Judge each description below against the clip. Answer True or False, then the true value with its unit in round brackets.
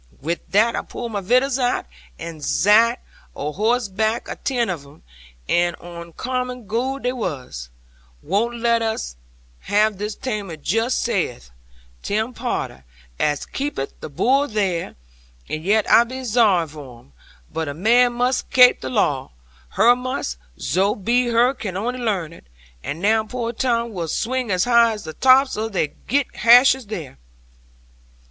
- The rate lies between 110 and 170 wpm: True (155 wpm)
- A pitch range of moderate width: False (6.3 semitones)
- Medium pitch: False (220 Hz)